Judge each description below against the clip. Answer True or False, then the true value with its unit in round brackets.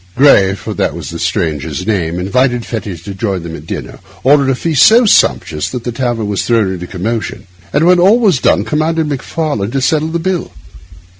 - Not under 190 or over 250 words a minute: True (200 wpm)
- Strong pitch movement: True (8.1 semitones)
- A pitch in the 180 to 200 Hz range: False (120 Hz)